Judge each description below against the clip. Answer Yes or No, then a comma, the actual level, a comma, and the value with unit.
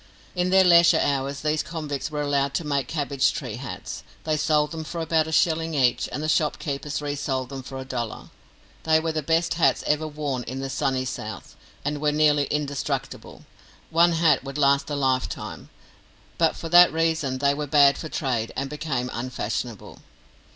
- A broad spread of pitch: No, average, 2.7 semitones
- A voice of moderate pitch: Yes, medium, 145 Hz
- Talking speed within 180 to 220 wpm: Yes, average, 185 wpm